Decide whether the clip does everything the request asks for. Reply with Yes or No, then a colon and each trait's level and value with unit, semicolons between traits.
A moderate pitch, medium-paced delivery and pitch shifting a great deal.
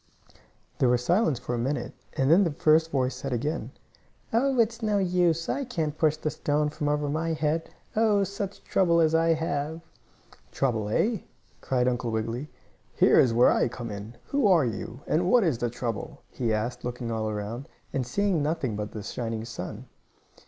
Yes: medium, 145 Hz; average, 185 wpm; wide, 5.7 semitones